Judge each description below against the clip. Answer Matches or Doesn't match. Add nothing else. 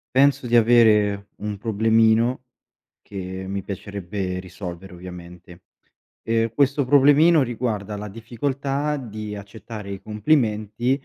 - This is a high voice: Doesn't match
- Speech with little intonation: Doesn't match